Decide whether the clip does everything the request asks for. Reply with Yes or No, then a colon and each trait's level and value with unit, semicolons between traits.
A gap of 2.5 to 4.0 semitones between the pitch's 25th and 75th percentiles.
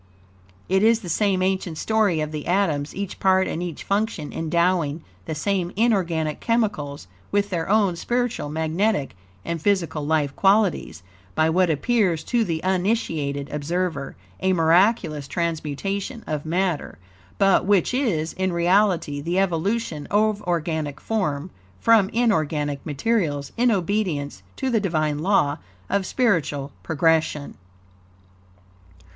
No: average, 4.6 semitones